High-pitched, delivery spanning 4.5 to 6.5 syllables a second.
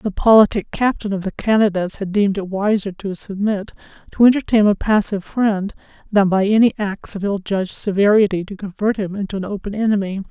Yes: high, 200 Hz; 5.8 syllables/s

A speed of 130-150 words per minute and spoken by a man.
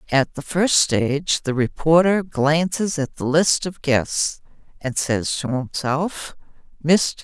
No: average, 140 wpm; female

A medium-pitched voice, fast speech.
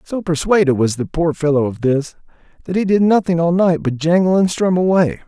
Yes: medium, 165 Hz; fast, 215 wpm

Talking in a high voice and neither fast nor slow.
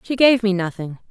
No: high, 210 Hz; fast, 215 wpm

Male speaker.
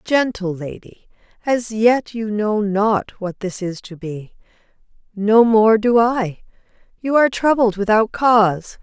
No: female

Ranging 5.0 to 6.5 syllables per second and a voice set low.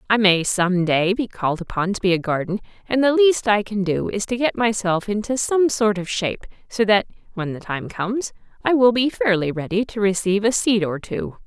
No: 5.3 syllables/s; high, 205 Hz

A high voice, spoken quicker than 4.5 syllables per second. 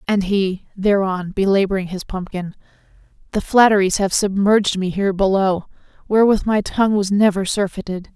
Yes: high, 195 Hz; 5.4 syllables/s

